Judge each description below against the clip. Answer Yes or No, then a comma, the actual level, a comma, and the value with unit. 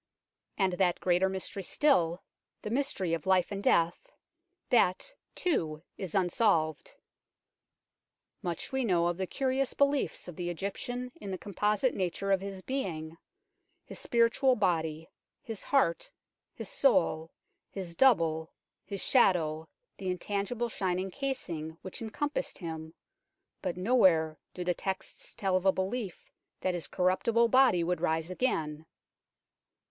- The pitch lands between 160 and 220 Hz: Yes, medium, 185 Hz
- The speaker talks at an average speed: No, slow, 130 wpm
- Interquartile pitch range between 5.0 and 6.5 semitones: Yes, wide, 5.4 semitones